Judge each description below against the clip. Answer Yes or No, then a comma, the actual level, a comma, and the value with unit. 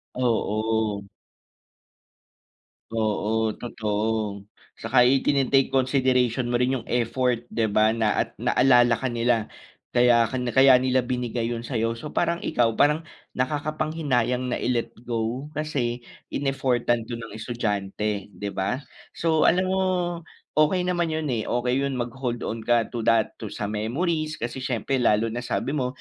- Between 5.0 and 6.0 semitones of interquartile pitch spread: No, average, 2.9 semitones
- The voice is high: No, low, 120 Hz